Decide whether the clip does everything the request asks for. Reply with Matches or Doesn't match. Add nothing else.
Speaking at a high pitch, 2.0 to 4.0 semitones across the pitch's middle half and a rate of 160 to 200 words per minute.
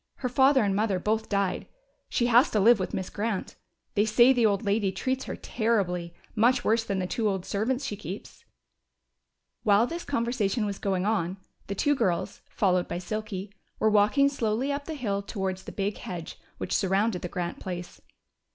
Matches